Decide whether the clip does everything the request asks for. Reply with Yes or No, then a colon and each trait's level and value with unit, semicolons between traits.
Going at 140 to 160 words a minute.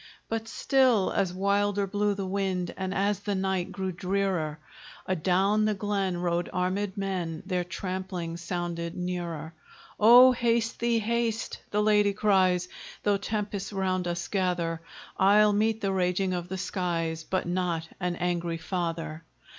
Yes: average, 145 wpm